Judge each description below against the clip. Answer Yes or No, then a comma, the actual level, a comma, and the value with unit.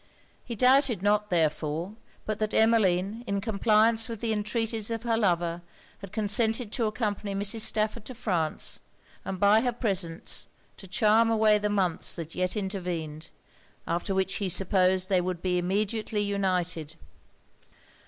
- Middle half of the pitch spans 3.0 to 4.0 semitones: Yes, average, 3.4 semitones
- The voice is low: No, high, 205 Hz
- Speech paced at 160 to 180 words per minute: No, average, 145 wpm